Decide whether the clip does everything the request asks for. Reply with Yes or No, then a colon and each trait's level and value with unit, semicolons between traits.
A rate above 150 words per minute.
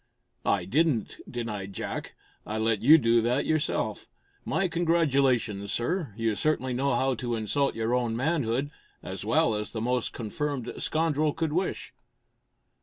No: average, 145 wpm